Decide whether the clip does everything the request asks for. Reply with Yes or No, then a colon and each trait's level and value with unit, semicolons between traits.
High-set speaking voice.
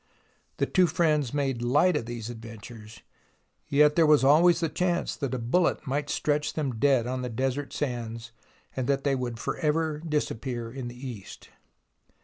No: low, 135 Hz